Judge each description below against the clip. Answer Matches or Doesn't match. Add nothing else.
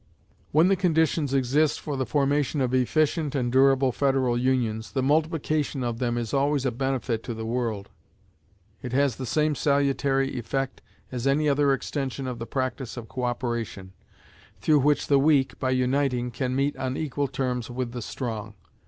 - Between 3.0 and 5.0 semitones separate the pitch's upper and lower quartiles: Doesn't match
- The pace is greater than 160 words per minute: Matches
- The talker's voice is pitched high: Doesn't match